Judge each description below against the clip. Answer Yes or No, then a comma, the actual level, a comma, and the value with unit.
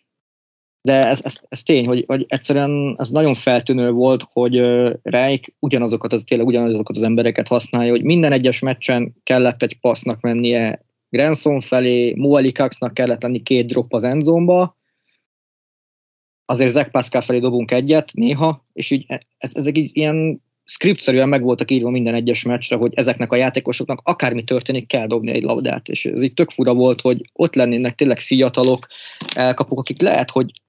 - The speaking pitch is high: No, low, 125 Hz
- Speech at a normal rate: No, fast, 165 wpm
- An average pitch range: No, narrow, 2.2 semitones